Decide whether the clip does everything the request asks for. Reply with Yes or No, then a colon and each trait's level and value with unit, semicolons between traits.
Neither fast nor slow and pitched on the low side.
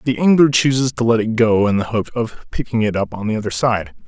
No: fast, 265 wpm; low, 115 Hz